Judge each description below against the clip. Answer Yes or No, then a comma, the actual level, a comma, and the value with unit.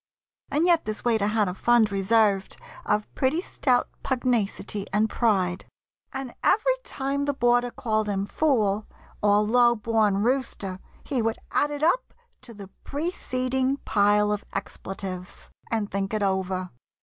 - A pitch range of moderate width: Yes, average, 4.3 semitones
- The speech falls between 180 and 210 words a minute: No, average, 145 wpm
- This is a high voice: Yes, high, 220 Hz